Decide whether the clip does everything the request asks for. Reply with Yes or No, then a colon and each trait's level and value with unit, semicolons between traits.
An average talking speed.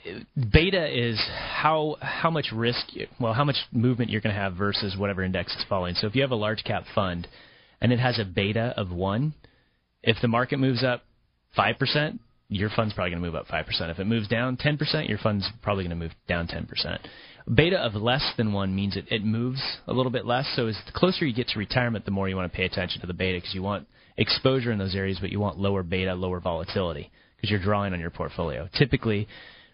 No: fast, 240 wpm